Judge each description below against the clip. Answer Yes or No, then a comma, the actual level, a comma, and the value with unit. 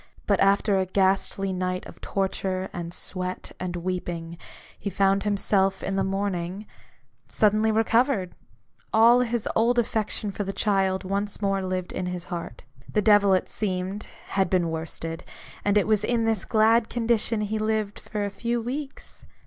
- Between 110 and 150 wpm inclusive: No, average, 165 wpm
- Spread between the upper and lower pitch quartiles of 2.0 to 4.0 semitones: Yes, average, 2.7 semitones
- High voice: Yes, high, 195 Hz